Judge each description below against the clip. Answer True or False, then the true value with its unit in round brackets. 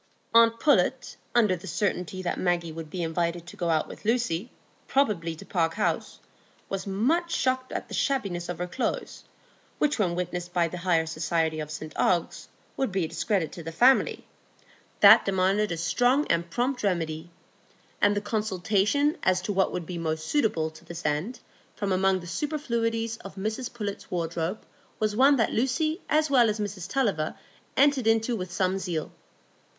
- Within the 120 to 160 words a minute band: False (175 wpm)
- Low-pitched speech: False (190 Hz)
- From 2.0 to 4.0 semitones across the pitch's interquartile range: False (5.2 semitones)